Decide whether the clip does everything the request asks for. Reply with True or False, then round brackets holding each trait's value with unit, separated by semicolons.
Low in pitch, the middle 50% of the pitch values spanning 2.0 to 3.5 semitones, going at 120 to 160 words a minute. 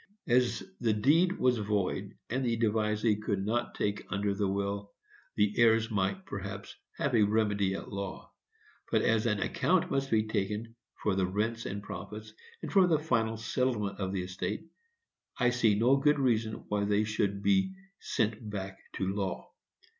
False (110 Hz; 3.0 semitones; 170 wpm)